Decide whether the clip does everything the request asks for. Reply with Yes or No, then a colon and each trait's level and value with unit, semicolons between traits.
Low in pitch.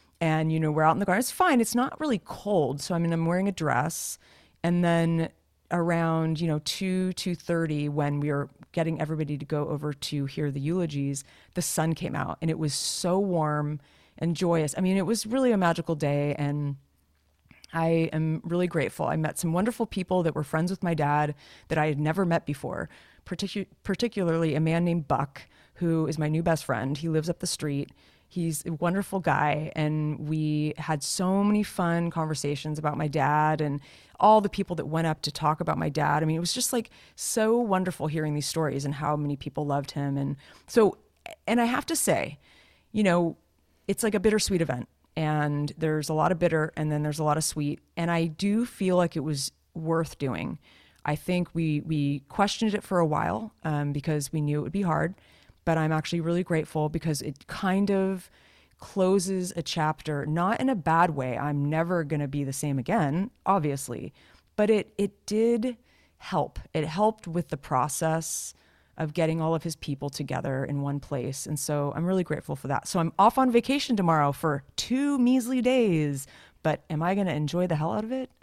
No: medium, 160 Hz